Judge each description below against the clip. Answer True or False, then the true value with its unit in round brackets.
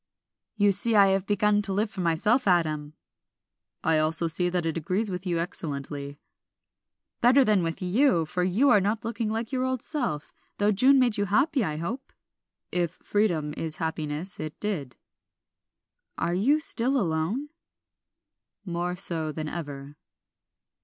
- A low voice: False (185 Hz)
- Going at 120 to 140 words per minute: False (155 wpm)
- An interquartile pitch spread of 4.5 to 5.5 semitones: True (5.2 semitones)